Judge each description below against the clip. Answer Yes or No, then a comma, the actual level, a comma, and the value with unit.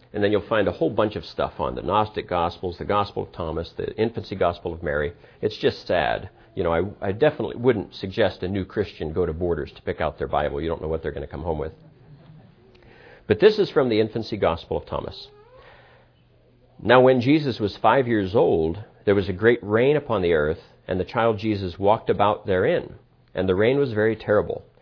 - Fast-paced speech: Yes, fast, 220 wpm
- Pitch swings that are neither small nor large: No, wide, 6.1 semitones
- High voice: No, low, 105 Hz